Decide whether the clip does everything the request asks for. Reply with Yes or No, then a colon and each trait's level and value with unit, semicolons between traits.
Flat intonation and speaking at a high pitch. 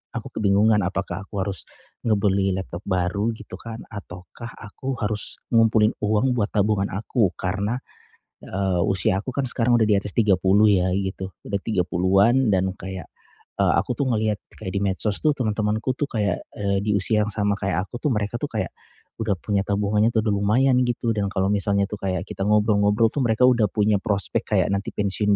No: narrow, 2.3 semitones; low, 105 Hz